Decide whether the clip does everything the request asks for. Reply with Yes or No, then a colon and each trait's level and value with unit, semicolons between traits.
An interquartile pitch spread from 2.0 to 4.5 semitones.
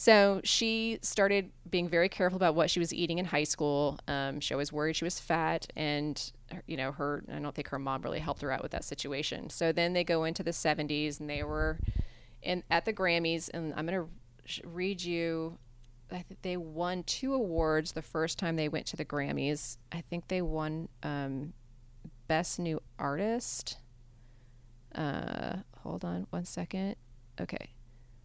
Yes: average, 3.9 semitones